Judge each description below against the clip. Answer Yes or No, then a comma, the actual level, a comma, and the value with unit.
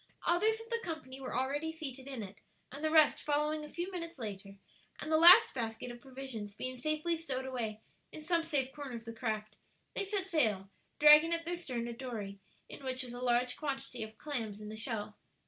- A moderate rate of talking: No, fast, 210 wpm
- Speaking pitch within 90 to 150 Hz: No, very high, 265 Hz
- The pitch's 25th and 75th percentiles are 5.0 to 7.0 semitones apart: Yes, wide, 5.5 semitones